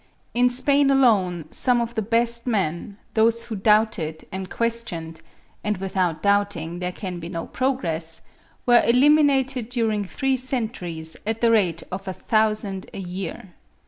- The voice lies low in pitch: No, high, 215 Hz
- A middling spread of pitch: Yes, average, 4.9 semitones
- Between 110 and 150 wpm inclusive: Yes, average, 140 wpm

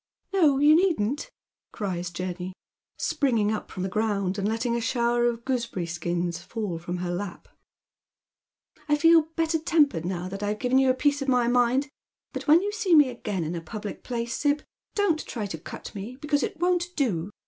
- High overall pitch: Yes, high, 235 Hz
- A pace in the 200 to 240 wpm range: Yes, fast, 205 wpm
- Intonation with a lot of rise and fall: Yes, wide, 7.6 semitones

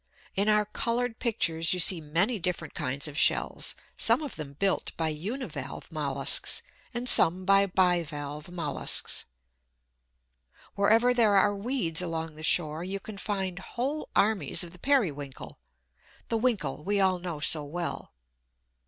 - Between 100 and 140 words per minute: No, average, 150 wpm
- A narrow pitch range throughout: No, average, 4.9 semitones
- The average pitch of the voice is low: No, medium, 185 Hz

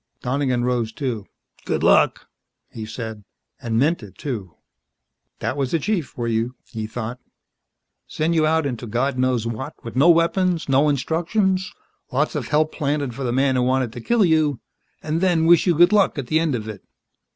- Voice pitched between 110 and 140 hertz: Yes, low, 135 Hz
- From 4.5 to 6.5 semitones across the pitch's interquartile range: Yes, average, 5.1 semitones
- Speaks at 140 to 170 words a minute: No, average, 185 wpm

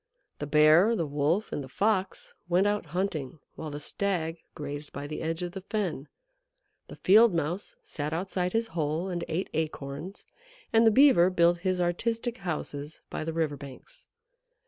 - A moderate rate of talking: Yes, average, 170 wpm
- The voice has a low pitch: No, medium, 170 Hz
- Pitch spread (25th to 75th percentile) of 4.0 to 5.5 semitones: Yes, average, 4.3 semitones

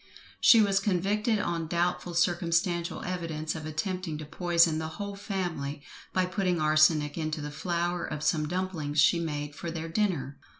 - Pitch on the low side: No, medium, 170 Hz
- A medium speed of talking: Yes, average, 160 wpm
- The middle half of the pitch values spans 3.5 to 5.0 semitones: No, average, 2.9 semitones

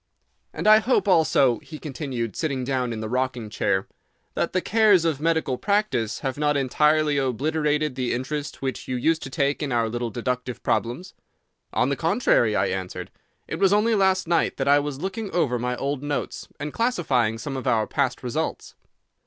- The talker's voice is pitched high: No, medium, 140 Hz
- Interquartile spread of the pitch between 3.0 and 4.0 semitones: No, average, 4.7 semitones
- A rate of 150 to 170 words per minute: No, average, 185 wpm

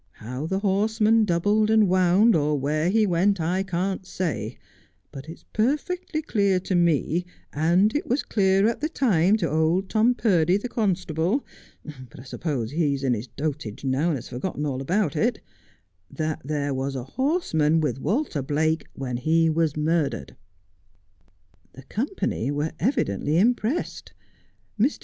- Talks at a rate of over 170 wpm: No, average, 160 wpm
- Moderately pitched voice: Yes, medium, 170 Hz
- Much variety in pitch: Yes, wide, 6.1 semitones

